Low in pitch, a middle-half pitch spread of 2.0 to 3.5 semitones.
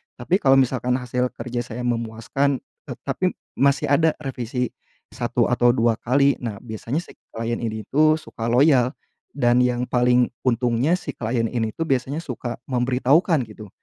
Yes: low, 125 Hz; average, 2.7 semitones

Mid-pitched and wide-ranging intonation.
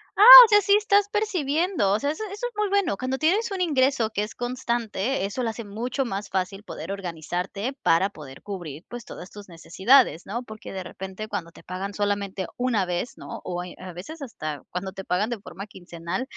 No: high, 210 Hz; wide, 6.5 semitones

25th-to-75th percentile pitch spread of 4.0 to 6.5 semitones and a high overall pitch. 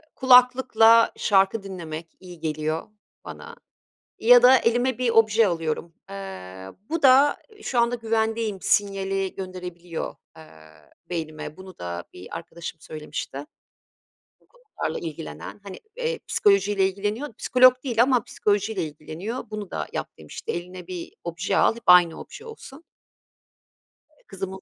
Yes: wide, 5.5 semitones; high, 195 Hz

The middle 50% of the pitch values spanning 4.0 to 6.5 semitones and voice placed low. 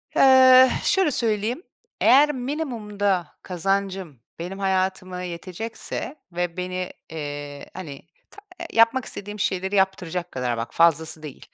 No: average, 5.1 semitones; high, 190 Hz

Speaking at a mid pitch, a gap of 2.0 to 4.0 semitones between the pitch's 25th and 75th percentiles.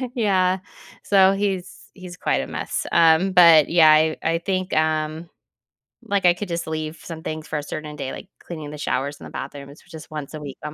Yes: medium, 160 Hz; average, 2.9 semitones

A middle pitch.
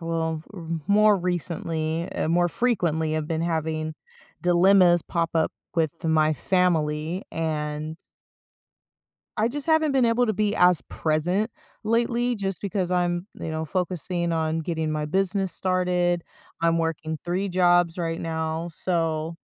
Yes: medium, 170 Hz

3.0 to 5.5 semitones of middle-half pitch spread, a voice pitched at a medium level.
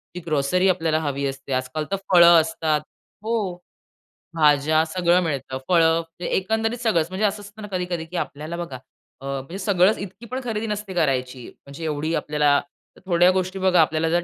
Yes: average, 3.6 semitones; medium, 170 Hz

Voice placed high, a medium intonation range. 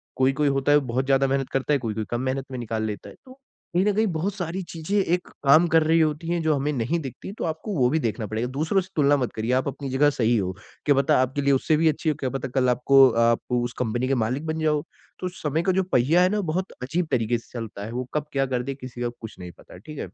No: low, 135 Hz; average, 4.3 semitones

